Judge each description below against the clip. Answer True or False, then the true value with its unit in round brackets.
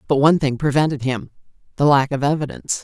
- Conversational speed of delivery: True (170 wpm)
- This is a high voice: False (140 Hz)